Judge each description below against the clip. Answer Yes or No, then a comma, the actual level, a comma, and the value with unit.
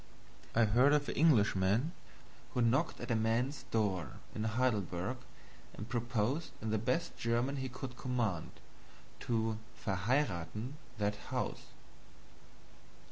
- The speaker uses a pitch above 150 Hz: No, low, 115 Hz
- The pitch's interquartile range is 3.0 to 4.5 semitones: Yes, average, 3.5 semitones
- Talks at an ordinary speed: No, slow, 120 wpm